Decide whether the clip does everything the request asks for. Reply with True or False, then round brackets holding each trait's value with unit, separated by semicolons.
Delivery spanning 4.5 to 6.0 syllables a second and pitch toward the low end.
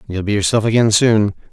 True (5.8 syllables/s; 105 Hz)